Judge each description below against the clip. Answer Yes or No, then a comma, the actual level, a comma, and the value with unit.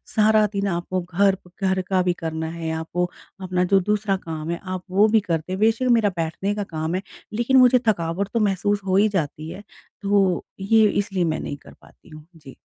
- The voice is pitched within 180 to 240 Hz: Yes, high, 190 Hz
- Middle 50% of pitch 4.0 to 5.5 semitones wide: No, average, 3.5 semitones